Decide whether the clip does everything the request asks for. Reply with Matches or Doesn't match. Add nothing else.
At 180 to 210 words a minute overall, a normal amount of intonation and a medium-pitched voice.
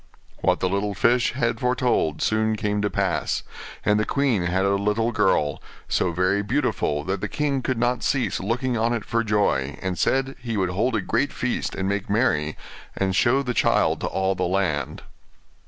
Doesn't match